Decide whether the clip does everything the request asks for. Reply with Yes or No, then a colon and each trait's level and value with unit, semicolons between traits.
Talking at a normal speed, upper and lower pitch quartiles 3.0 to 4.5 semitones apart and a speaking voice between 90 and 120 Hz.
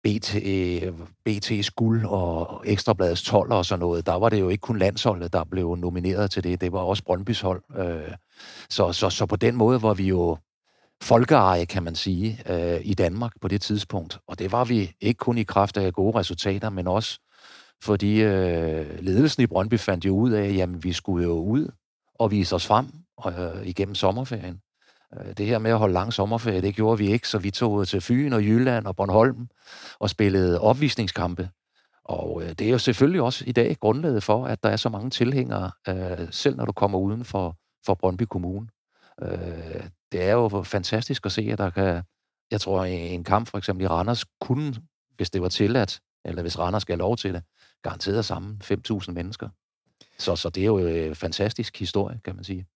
Yes: average, 195 wpm; average, 3.5 semitones; low, 100 Hz